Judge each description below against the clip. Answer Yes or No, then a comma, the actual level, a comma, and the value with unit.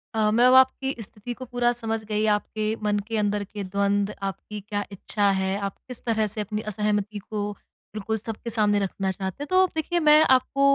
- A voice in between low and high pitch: No, high, 210 Hz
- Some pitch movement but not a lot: No, narrow, 2.3 semitones